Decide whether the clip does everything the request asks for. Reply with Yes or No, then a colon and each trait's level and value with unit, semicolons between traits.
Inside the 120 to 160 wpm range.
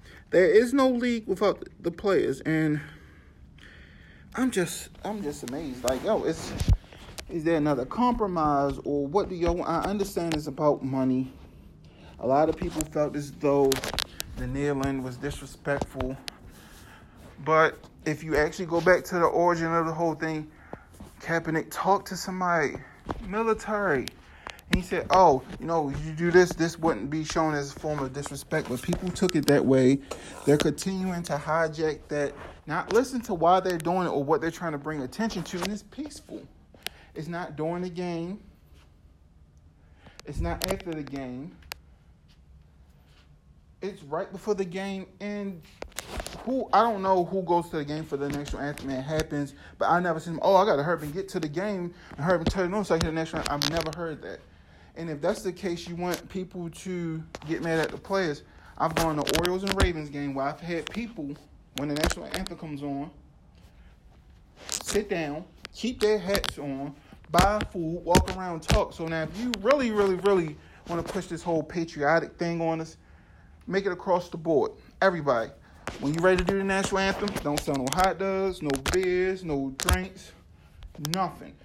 No: average, 185 wpm